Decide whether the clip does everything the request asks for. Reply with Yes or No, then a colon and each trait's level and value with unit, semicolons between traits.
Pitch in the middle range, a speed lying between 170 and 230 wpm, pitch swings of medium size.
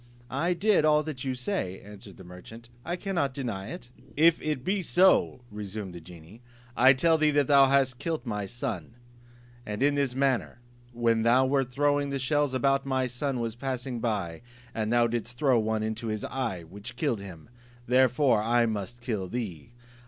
No: low, 125 Hz; average, 180 wpm; average, 4.3 semitones